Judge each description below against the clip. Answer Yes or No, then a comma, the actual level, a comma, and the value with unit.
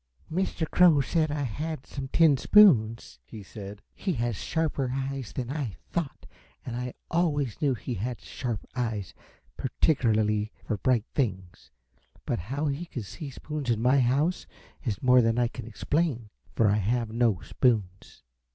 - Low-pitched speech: Yes, low, 125 Hz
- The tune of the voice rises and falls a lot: No, average, 4.8 semitones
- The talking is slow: No, average, 160 wpm